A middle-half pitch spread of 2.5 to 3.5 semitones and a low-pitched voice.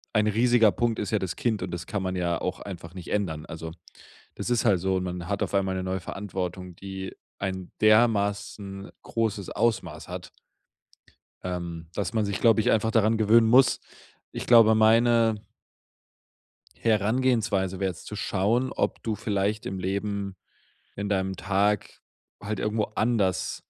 Yes: average, 2.9 semitones; low, 100 Hz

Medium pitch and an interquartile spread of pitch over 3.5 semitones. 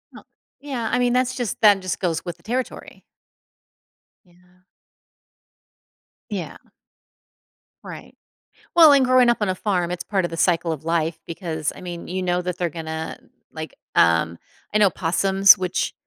Yes: medium, 180 Hz; average, 4.0 semitones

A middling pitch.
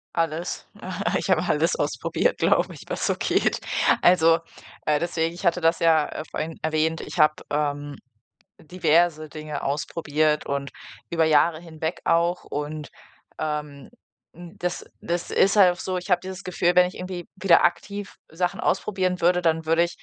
Yes: medium, 165 Hz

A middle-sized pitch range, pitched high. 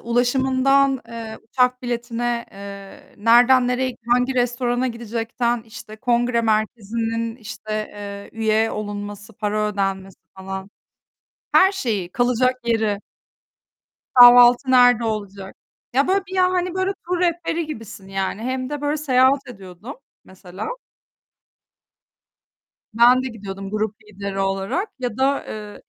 Yes: average, 3.6 semitones; high, 235 Hz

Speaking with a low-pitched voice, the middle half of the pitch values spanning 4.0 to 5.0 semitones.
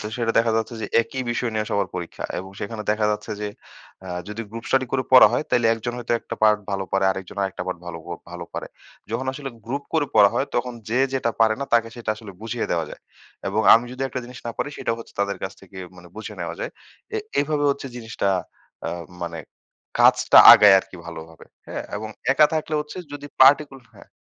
Yes: low, 115 Hz; average, 4.4 semitones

